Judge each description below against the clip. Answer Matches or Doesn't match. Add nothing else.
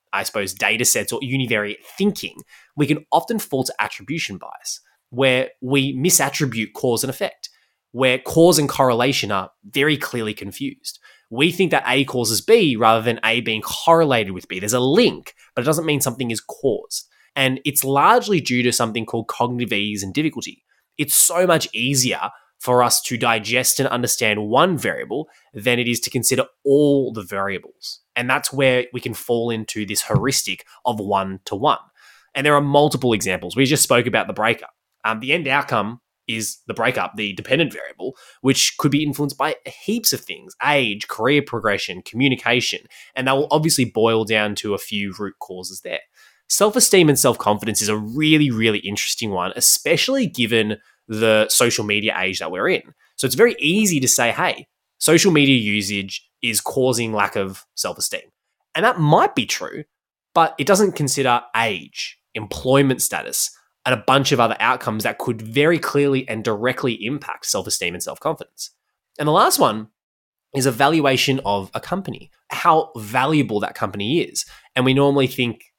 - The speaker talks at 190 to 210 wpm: Doesn't match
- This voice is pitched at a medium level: Doesn't match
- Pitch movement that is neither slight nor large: Matches